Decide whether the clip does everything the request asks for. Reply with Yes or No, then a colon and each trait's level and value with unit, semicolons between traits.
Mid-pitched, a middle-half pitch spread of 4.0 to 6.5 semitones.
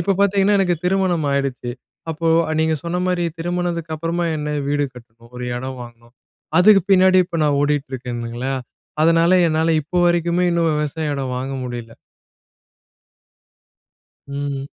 Yes: medium, 155 Hz; average, 4.7 semitones